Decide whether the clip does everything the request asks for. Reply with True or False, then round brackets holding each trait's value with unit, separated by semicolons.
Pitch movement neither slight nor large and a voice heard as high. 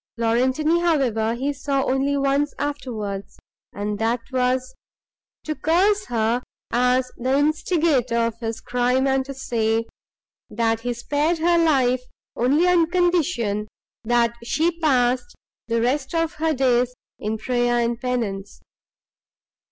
True (4.0 semitones; 255 Hz)